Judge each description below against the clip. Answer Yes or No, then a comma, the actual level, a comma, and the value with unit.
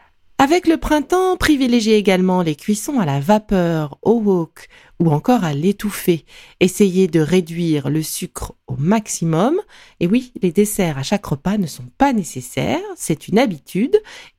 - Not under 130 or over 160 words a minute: Yes, average, 155 wpm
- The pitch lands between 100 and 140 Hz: No, high, 195 Hz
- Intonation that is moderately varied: No, wide, 7.0 semitones